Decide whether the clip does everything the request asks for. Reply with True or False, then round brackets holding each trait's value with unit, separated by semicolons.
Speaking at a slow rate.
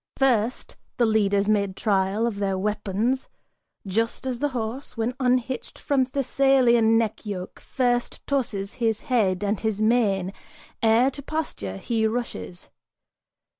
True (130 wpm)